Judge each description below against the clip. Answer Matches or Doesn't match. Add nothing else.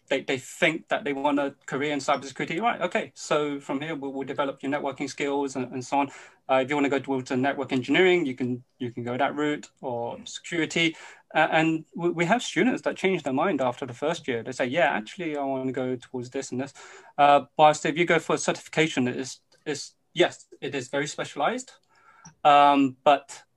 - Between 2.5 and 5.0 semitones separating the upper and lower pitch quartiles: Matches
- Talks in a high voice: Doesn't match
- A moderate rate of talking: Doesn't match